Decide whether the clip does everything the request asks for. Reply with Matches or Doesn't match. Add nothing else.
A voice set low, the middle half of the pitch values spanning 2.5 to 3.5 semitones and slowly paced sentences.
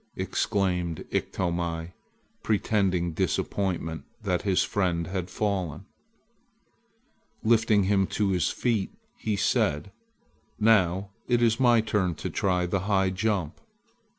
Matches